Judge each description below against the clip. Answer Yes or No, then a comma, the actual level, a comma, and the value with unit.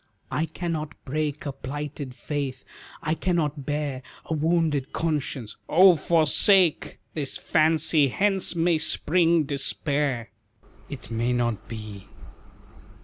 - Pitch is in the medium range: Yes, medium, 150 Hz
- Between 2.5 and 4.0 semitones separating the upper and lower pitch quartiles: Yes, average, 3.3 semitones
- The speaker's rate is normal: No, slow, 110 wpm